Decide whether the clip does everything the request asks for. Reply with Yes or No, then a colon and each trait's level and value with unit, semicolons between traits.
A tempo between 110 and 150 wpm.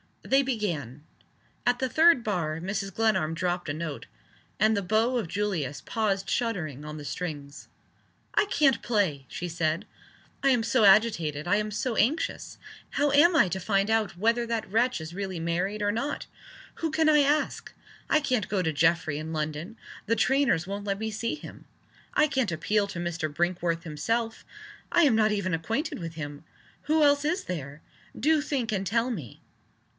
No: average, 180 wpm